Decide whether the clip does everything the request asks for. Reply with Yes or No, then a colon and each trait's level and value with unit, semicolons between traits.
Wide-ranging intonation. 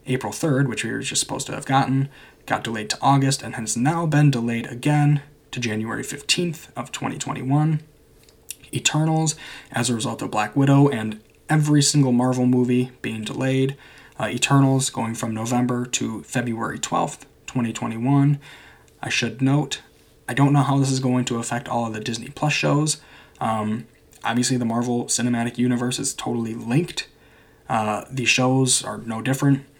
No: average, 3.0 semitones